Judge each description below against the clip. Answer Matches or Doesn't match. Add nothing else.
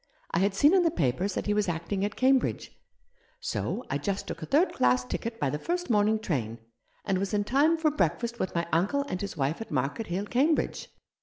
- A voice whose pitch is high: Matches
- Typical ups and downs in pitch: Doesn't match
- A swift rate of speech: Matches